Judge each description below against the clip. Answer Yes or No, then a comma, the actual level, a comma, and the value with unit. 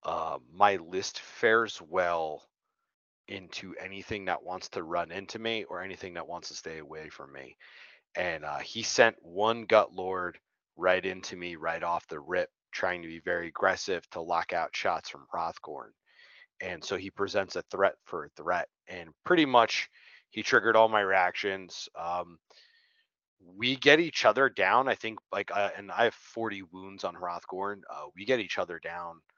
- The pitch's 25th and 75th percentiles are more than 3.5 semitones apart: Yes, average, 4.6 semitones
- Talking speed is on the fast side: No, average, 180 wpm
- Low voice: Yes, very low, 95 Hz